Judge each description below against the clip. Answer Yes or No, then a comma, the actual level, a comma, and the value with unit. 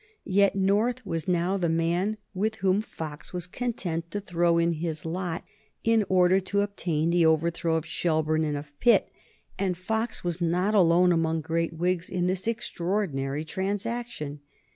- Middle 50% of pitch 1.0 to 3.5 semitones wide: Yes, average, 3.2 semitones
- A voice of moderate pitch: Yes, medium, 175 Hz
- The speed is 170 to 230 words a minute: No, average, 160 wpm